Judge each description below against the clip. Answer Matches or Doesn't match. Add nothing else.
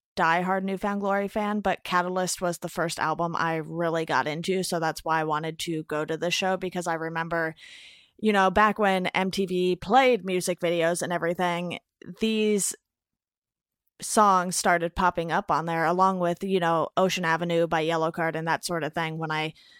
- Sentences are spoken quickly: Doesn't match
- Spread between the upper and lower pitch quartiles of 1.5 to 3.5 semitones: Matches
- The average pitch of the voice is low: Doesn't match